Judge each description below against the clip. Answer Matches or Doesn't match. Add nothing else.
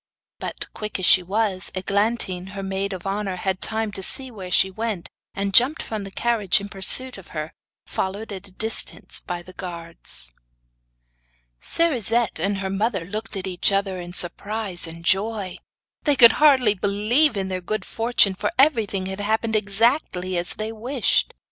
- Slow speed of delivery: Doesn't match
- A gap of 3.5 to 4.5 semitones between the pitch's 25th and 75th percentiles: Doesn't match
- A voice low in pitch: Doesn't match